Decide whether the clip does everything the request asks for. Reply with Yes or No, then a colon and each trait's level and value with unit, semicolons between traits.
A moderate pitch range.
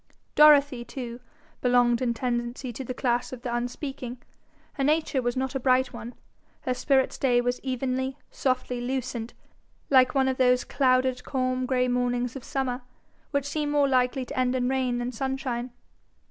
No: narrow, 1.4 semitones